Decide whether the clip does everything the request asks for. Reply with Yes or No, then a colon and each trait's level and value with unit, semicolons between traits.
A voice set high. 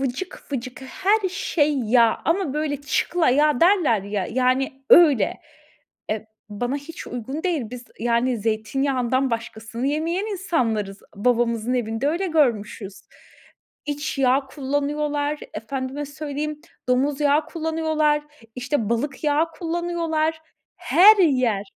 Yes: very high, 280 Hz